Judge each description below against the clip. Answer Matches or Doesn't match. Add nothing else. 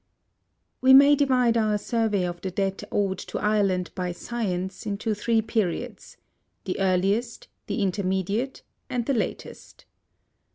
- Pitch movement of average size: Matches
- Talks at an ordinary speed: Doesn't match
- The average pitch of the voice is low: Doesn't match